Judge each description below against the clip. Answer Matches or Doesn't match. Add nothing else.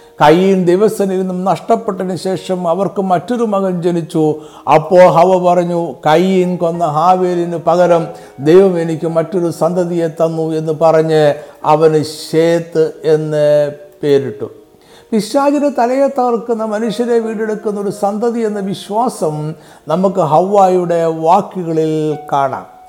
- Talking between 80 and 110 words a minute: Matches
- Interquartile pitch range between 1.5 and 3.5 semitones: Doesn't match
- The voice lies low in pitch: Doesn't match